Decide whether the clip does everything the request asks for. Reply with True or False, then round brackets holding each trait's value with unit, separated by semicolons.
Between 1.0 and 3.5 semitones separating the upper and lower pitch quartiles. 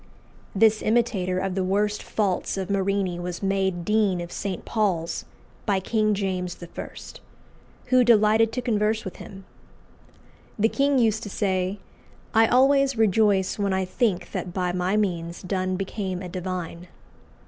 True (2.9 semitones)